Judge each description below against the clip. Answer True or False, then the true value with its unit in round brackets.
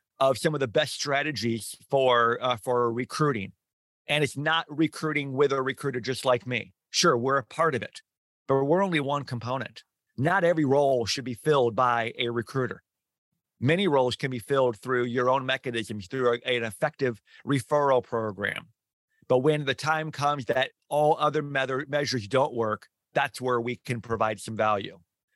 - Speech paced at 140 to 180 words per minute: True (175 wpm)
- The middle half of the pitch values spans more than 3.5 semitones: False (3.1 semitones)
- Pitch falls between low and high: False (130 Hz)